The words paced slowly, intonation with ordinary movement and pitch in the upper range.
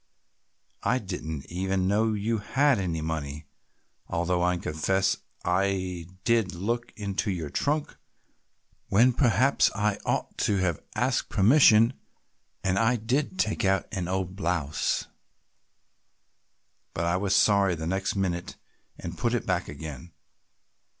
No: slow, 130 wpm; average, 4.2 semitones; very low, 95 Hz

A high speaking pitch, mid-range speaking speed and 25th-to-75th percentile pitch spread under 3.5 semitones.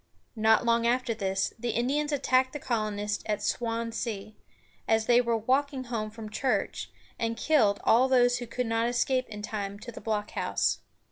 Yes: high, 230 Hz; average, 165 wpm; average, 2.7 semitones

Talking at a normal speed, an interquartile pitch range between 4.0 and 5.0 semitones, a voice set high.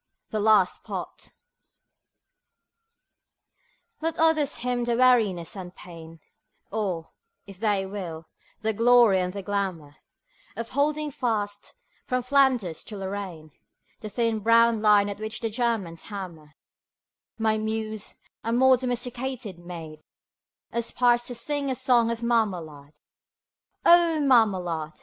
No: slow, 120 wpm; average, 4.6 semitones; high, 220 Hz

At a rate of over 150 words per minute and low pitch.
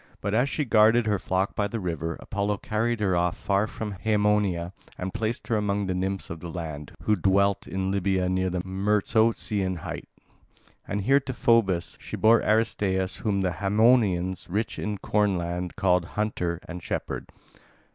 Yes: average, 170 wpm; low, 100 Hz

